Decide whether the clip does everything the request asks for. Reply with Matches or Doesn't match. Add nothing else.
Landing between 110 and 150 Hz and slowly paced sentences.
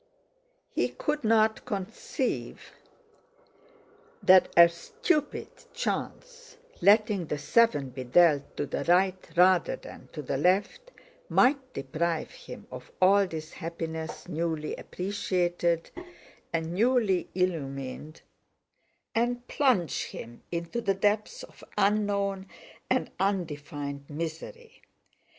Doesn't match